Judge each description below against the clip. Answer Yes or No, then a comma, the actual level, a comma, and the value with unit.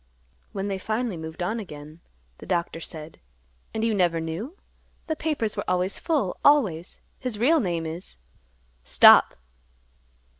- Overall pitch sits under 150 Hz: No, high, 190 Hz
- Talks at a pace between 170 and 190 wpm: No, average, 140 wpm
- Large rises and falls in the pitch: Yes, wide, 5.8 semitones